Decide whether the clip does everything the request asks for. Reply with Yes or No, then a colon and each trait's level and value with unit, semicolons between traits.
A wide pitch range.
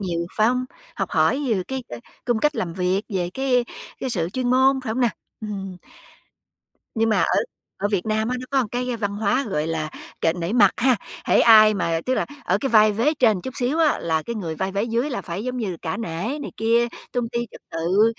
No: average, 5.0 semitones